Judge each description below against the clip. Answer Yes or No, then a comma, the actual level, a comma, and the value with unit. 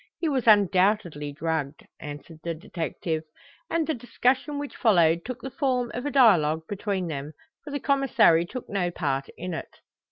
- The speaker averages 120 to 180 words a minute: Yes, average, 165 wpm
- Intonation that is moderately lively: No, wide, 7.8 semitones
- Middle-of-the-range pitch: No, high, 195 Hz